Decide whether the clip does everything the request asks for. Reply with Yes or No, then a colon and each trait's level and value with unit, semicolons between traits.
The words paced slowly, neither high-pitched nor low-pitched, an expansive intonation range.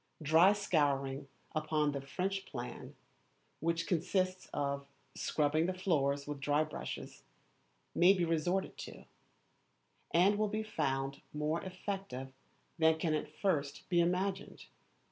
No: slow, 125 wpm; medium, 160 Hz; average, 4.4 semitones